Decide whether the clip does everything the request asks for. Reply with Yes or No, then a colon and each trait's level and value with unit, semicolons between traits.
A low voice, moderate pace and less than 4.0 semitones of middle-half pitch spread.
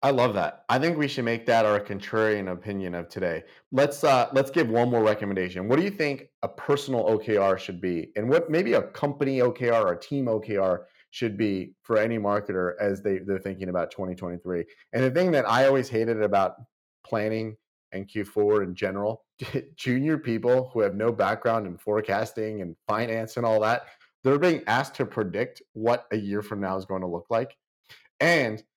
No: low, 110 Hz; average, 195 wpm; average, 4.5 semitones